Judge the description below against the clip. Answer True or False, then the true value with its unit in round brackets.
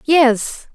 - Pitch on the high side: True (270 Hz)